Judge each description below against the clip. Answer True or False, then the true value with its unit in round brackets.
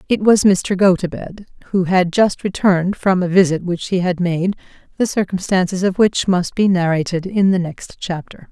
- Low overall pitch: False (185 Hz)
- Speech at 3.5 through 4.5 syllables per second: False (4.9 syllables/s)